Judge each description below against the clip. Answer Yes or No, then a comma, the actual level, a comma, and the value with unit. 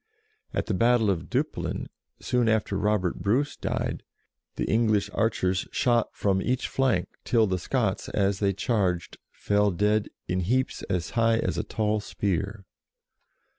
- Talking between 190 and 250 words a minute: No, average, 150 wpm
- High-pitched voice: No, low, 105 Hz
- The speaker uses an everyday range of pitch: Yes, average, 3.1 semitones